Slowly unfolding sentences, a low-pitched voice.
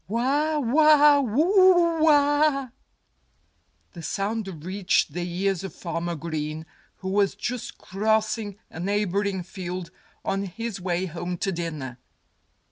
No: slow, 120 wpm; high, 200 Hz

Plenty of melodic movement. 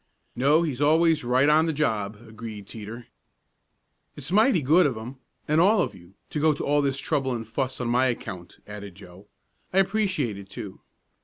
Yes: wide, 6.1 semitones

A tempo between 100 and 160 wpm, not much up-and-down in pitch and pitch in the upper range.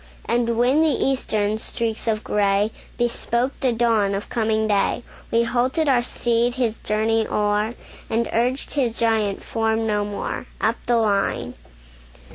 Yes: average, 145 wpm; narrow, 2.1 semitones; high, 225 Hz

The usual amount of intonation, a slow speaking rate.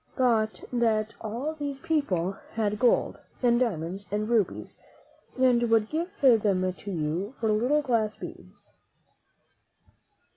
Yes: average, 3.7 semitones; slow, 125 wpm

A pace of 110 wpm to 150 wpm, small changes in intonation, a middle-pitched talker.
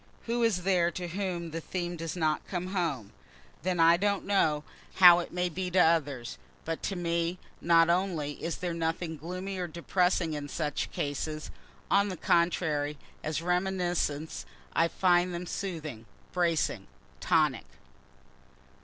Yes: average, 145 wpm; narrow, 2.3 semitones; medium, 170 Hz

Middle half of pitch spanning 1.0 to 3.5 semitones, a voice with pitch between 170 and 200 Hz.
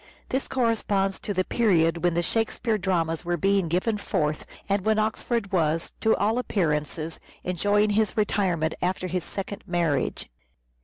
No: average, 4.1 semitones; high, 190 Hz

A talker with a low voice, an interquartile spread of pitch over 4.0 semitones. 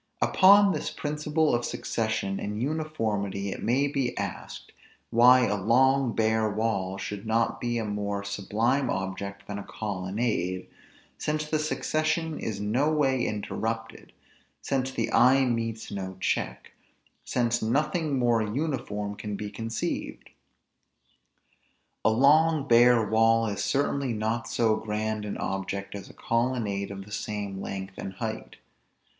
Yes: low, 115 Hz; average, 4.5 semitones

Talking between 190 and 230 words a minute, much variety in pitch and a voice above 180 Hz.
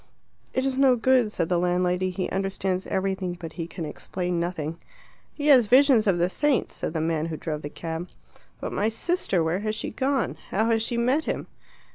Yes: average, 200 wpm; wide, 5.8 semitones; high, 190 Hz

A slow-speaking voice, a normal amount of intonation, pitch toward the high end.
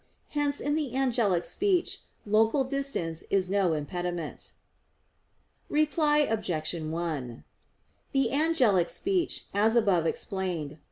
No: slow, 110 wpm; wide, 8.5 semitones; high, 205 Hz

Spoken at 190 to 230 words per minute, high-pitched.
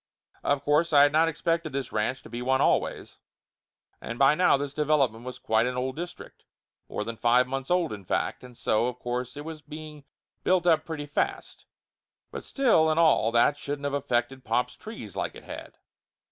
No: average, 195 wpm; medium, 140 Hz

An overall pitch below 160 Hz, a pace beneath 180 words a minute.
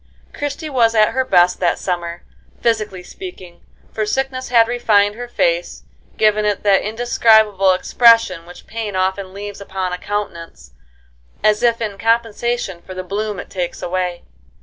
No: high, 210 Hz; average, 150 wpm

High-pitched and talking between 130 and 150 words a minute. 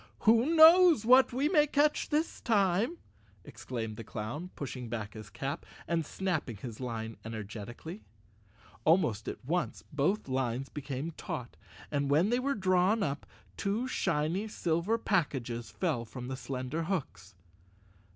No: medium, 155 Hz; average, 140 wpm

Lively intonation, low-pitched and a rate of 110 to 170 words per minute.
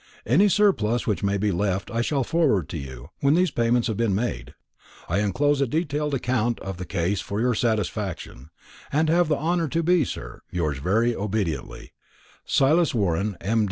No: wide, 7.1 semitones; low, 115 Hz; average, 180 wpm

